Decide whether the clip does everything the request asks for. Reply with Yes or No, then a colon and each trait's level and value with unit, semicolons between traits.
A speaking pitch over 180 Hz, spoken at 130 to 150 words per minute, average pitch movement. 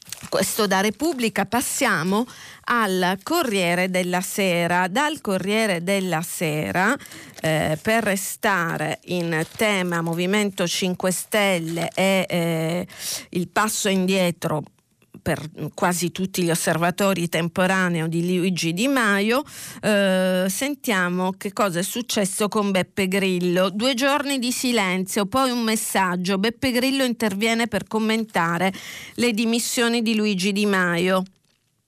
No: high, 190 Hz; slow, 115 wpm; average, 3.8 semitones